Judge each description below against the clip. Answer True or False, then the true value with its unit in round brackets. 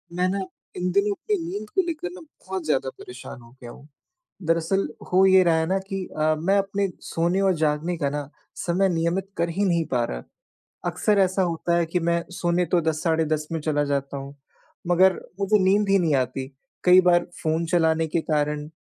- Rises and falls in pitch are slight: False (3.5 semitones)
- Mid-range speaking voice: True (170 Hz)